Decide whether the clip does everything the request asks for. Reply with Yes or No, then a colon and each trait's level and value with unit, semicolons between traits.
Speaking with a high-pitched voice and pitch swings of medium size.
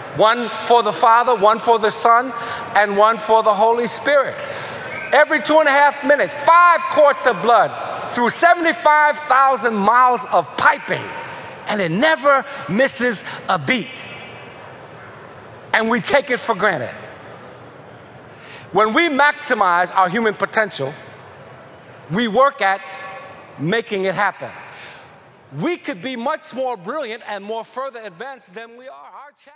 Yes: high, 235 Hz; average, 5.0 semitones